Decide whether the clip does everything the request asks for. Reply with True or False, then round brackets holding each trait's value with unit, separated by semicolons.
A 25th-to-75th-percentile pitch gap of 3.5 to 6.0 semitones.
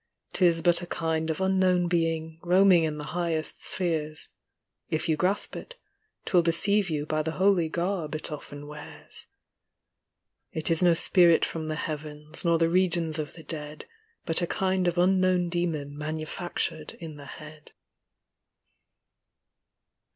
False (2.4 semitones)